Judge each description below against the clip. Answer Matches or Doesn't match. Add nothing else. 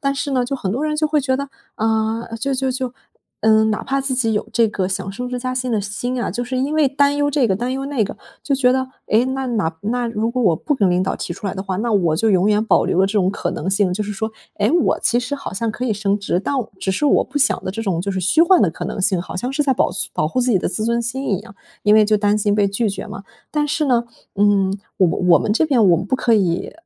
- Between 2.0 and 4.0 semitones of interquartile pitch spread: Doesn't match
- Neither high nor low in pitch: Doesn't match